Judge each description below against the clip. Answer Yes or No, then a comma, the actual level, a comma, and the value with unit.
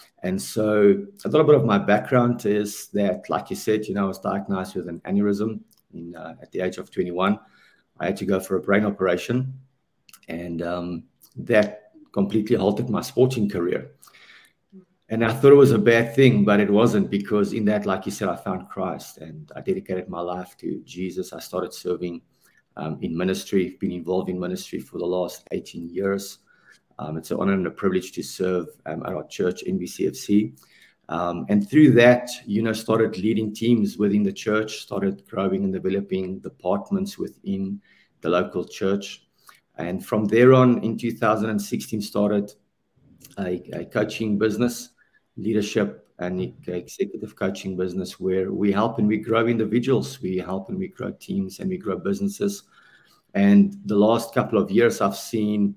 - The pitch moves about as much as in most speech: Yes, average, 4.4 semitones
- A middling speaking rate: Yes, average, 175 wpm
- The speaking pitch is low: Yes, low, 105 Hz